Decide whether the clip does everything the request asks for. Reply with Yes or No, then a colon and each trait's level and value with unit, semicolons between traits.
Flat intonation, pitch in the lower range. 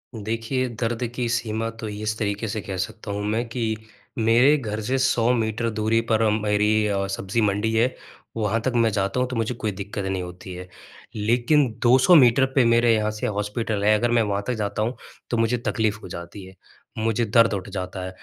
Yes: narrow, 2.3 semitones; low, 110 Hz